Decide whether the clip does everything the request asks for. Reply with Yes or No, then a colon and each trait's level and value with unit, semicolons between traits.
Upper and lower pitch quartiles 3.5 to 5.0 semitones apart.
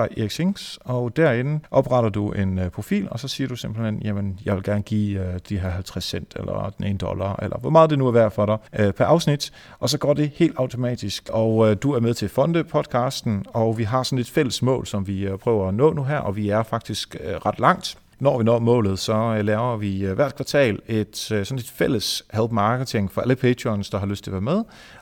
Yes: average, 4.3 semitones